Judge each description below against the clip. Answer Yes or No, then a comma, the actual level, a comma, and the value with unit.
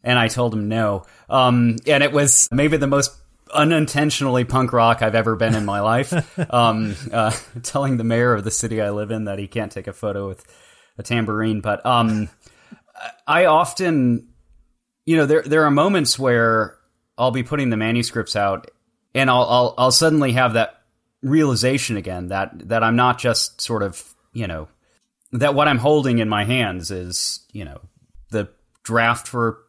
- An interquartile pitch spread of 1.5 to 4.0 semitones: Yes, average, 3.1 semitones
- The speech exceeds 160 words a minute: Yes, average, 180 wpm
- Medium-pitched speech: No, low, 115 Hz